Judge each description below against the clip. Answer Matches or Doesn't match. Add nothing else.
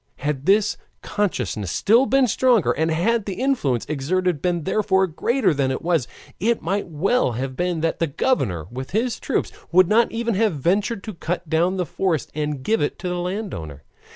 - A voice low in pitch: Doesn't match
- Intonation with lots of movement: Matches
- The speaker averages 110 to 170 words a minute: Doesn't match